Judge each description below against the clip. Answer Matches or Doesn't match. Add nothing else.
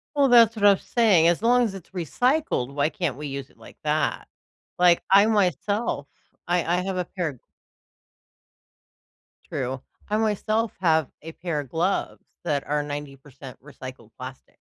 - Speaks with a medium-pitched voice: Matches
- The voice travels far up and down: Matches